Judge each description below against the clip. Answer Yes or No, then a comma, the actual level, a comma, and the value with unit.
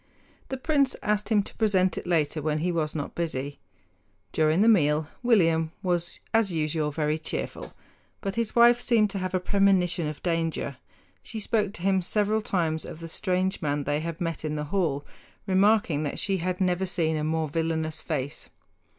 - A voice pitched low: No, medium, 170 Hz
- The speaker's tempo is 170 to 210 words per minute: Yes, average, 185 wpm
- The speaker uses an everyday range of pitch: Yes, average, 4.2 semitones